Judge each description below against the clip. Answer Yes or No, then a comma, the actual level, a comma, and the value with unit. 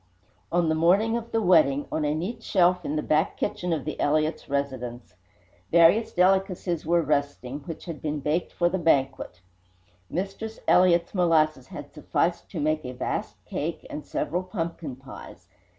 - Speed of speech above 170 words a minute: No, average, 165 wpm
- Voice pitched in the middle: Yes, medium, 165 Hz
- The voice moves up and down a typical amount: Yes, average, 3.5 semitones